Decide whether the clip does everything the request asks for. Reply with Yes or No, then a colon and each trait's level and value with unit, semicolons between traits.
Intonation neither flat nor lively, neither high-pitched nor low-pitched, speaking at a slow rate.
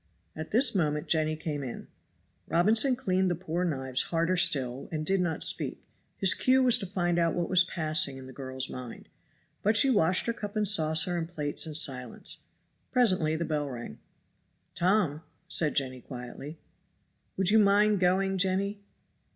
No: average, 4.5 semitones; medium, 170 Hz; average, 165 wpm